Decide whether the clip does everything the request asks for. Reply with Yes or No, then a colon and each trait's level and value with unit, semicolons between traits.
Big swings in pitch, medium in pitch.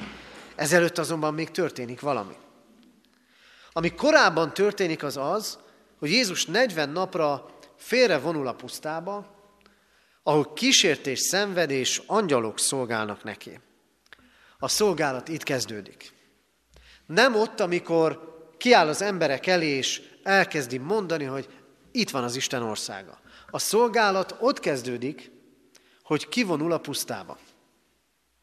Yes: wide, 6.7 semitones; medium, 160 Hz